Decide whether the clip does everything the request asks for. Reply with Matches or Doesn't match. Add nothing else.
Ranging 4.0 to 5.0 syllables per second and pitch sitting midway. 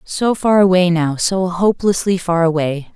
Matches